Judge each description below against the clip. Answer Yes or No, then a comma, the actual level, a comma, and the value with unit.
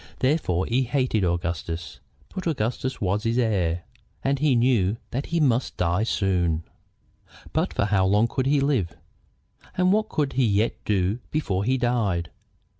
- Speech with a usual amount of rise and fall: No, wide, 6.2 semitones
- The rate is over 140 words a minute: Yes, average, 155 wpm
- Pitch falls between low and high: No, low, 115 Hz